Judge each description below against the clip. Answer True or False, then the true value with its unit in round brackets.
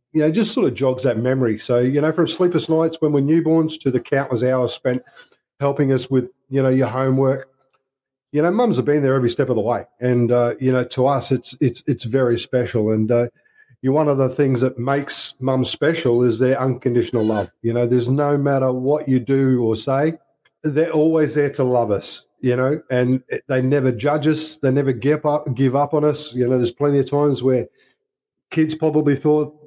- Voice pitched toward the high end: False (135 Hz)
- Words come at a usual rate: False (220 wpm)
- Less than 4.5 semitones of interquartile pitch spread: True (2.9 semitones)